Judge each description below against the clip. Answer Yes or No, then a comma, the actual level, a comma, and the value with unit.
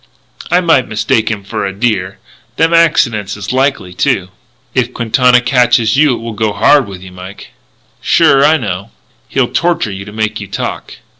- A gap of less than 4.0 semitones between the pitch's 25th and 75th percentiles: No, average, 5.0 semitones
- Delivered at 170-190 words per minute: Yes, average, 175 wpm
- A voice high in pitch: No, low, 115 Hz